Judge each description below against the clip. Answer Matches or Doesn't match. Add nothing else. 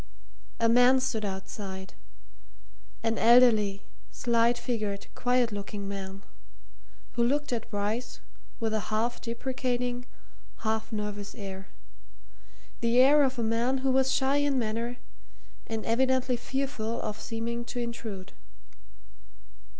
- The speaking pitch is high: Matches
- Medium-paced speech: Doesn't match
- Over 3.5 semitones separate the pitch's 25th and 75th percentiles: Doesn't match